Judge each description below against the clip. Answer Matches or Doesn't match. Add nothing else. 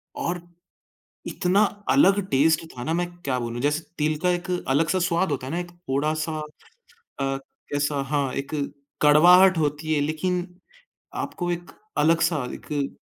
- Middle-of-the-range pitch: Matches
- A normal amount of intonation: Matches